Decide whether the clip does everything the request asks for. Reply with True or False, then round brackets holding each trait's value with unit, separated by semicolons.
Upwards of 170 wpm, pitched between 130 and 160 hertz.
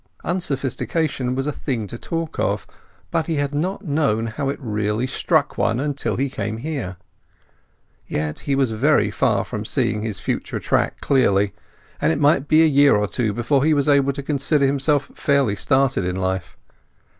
True (180 wpm; 135 Hz)